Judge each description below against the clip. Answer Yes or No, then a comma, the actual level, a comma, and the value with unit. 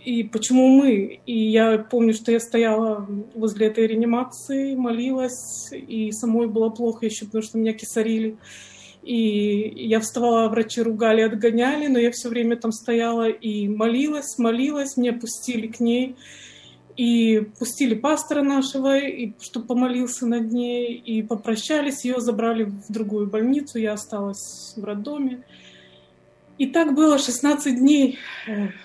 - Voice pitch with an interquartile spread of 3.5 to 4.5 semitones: No, narrow, 2.4 semitones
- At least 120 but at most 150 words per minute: Yes, average, 135 wpm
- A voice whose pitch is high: Yes, high, 235 Hz